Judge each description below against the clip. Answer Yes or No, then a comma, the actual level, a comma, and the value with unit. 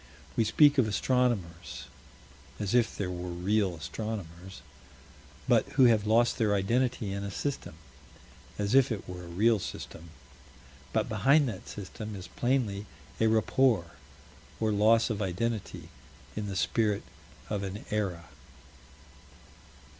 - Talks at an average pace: No, slow, 130 wpm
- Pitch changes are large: No, average, 3.5 semitones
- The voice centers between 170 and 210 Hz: No, low, 105 Hz